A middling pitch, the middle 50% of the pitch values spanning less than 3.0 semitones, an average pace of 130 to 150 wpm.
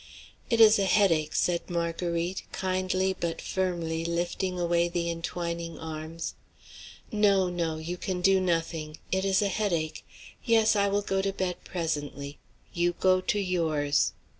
Yes: medium, 175 Hz; narrow, 2.4 semitones; average, 145 wpm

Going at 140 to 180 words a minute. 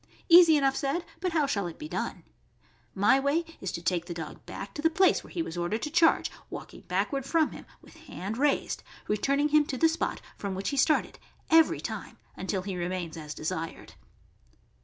No: average, 200 wpm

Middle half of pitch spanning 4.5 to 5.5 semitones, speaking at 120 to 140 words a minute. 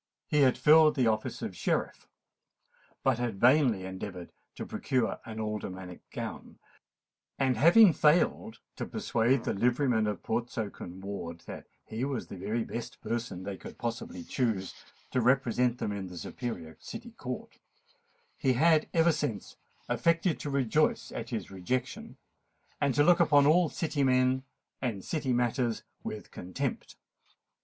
No: average, 5.1 semitones; average, 150 wpm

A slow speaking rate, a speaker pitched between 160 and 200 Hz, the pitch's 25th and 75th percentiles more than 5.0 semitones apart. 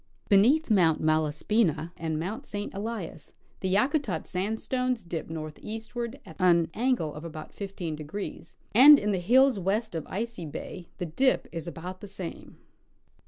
No: average, 155 wpm; high, 190 Hz; wide, 5.5 semitones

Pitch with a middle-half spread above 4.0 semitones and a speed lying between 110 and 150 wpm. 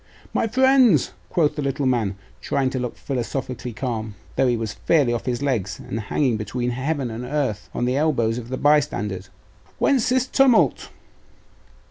No: average, 4.5 semitones; average, 165 wpm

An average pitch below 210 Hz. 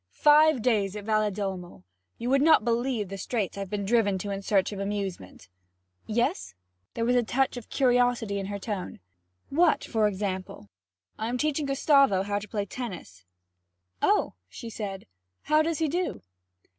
No: high, 215 Hz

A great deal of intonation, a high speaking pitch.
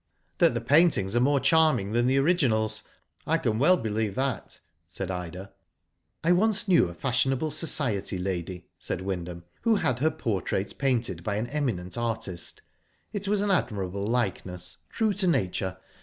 No: wide, 7.8 semitones; low, 115 Hz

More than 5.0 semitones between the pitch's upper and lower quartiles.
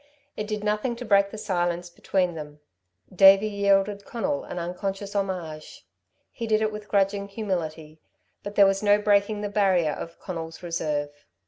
No: average, 3.2 semitones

